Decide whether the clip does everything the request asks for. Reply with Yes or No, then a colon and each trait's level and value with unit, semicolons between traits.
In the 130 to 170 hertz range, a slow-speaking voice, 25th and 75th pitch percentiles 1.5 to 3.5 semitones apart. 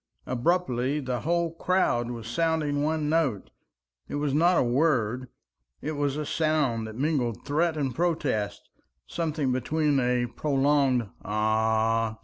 No: medium, 140 Hz; slow, 130 wpm; average, 4.7 semitones